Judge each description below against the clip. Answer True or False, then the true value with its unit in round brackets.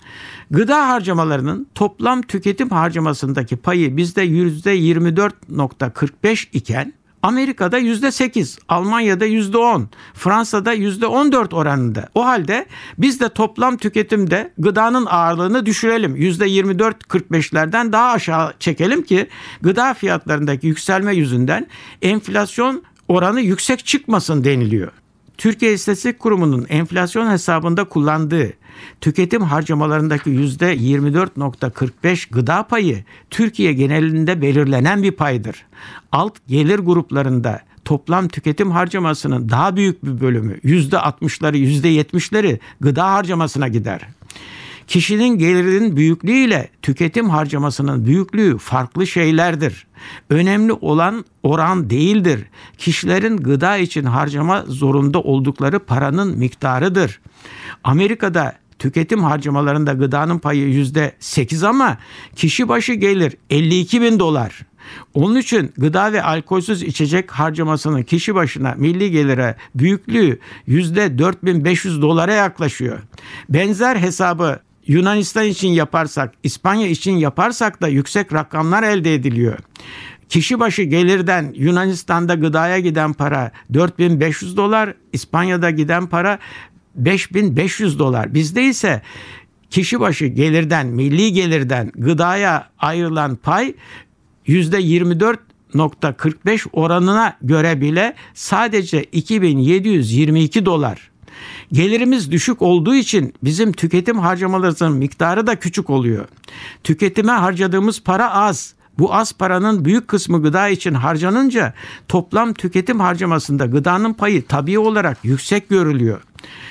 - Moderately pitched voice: True (170 Hz)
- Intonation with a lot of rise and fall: True (5.7 semitones)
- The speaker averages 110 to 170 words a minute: False (100 wpm)